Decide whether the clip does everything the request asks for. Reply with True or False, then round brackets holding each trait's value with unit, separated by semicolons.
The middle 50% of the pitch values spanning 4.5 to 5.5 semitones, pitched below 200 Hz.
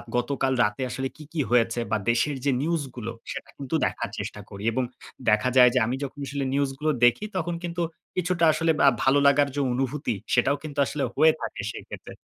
False (3.8 semitones; 140 Hz)